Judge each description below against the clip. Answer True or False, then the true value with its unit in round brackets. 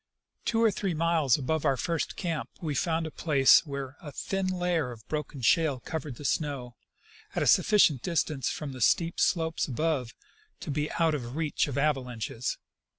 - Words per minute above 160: True (190 wpm)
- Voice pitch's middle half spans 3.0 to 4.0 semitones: True (3.7 semitones)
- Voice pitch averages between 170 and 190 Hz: False (150 Hz)